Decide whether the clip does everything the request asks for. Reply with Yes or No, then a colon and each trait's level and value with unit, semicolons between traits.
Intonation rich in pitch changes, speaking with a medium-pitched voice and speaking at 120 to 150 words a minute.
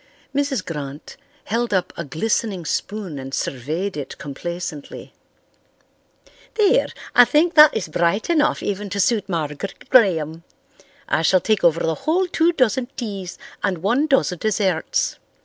No: wide, 6.8 semitones; high, 195 Hz; average, 140 wpm